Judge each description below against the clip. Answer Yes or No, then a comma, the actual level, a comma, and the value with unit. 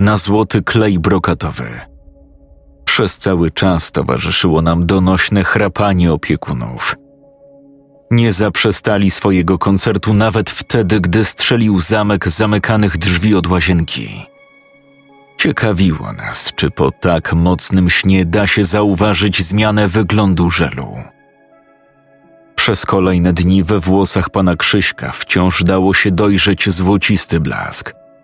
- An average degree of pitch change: Yes, average, 3.0 semitones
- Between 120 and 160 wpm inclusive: No, slow, 110 wpm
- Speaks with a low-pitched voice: Yes, low, 100 Hz